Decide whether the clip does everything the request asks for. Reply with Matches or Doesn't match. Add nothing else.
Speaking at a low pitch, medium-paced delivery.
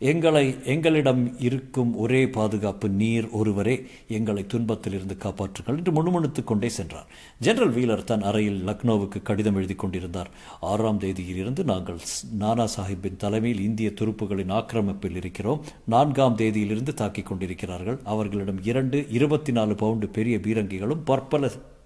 Matches